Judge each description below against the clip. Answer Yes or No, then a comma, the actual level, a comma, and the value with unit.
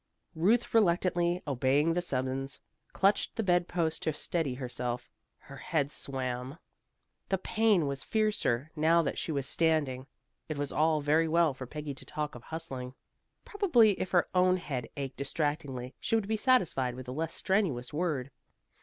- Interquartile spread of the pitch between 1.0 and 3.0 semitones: No, average, 4.8 semitones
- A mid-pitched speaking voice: Yes, medium, 155 Hz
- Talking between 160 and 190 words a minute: Yes, average, 165 wpm